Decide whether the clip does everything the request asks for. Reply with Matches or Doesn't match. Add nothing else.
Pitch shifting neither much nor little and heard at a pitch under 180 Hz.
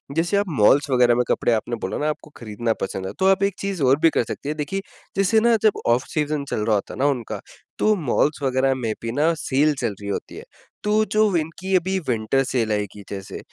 Doesn't match